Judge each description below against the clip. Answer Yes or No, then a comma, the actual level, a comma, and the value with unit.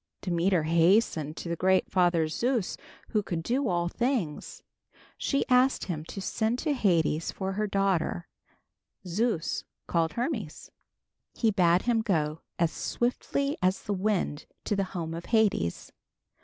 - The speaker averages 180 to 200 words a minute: No, average, 140 wpm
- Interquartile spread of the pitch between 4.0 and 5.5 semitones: Yes, average, 4.9 semitones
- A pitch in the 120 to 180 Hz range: No, high, 190 Hz